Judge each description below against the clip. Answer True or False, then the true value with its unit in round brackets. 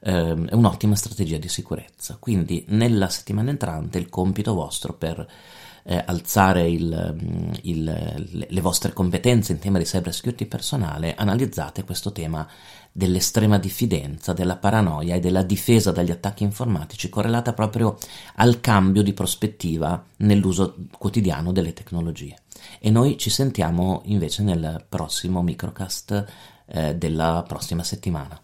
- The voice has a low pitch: True (95 Hz)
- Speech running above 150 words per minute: False (130 wpm)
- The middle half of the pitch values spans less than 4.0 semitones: True (3.3 semitones)